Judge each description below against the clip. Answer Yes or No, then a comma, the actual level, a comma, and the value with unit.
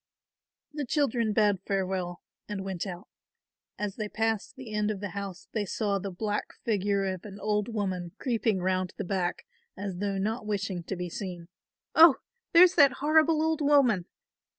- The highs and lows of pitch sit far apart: No, average, 3.2 semitones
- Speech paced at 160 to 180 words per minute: Yes, average, 170 wpm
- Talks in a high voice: Yes, high, 205 Hz